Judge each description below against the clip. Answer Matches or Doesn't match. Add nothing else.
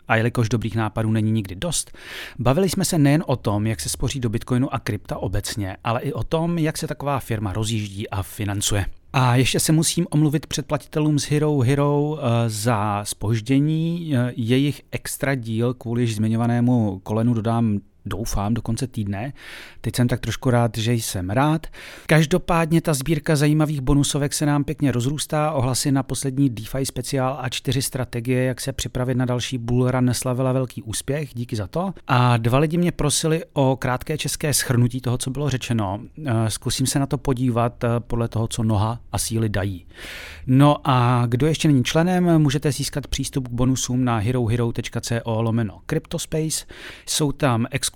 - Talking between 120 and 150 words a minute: Doesn't match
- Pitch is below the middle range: Matches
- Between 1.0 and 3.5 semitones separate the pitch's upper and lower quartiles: Doesn't match